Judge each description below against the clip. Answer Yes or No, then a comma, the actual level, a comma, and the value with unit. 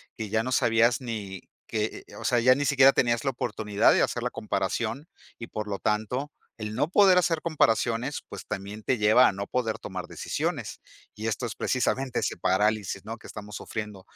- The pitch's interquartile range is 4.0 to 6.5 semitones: No, average, 3.3 semitones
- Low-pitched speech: Yes, low, 115 Hz